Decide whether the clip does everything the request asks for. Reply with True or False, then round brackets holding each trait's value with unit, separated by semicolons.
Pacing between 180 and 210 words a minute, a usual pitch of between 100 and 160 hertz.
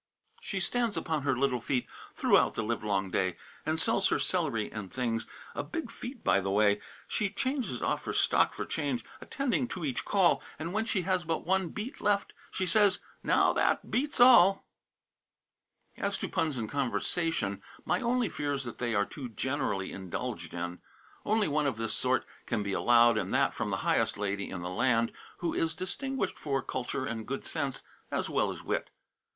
True (190 wpm; 140 Hz)